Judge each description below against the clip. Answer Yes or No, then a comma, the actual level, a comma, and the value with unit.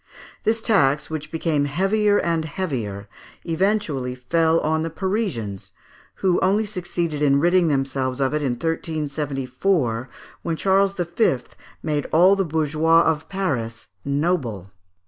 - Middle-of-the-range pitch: Yes, medium, 160 Hz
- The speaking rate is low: Yes, slow, 125 wpm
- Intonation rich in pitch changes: No, average, 5.0 semitones